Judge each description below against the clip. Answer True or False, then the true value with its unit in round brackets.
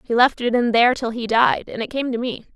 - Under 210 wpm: False (305 wpm)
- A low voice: False (235 Hz)